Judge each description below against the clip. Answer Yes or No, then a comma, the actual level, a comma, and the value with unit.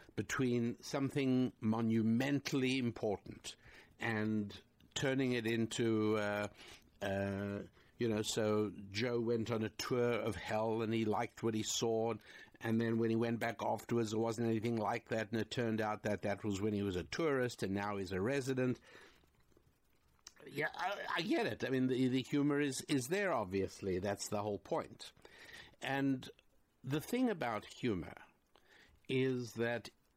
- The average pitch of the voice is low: Yes, low, 115 Hz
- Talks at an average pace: Yes, average, 160 wpm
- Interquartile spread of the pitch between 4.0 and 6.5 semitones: No, average, 3.2 semitones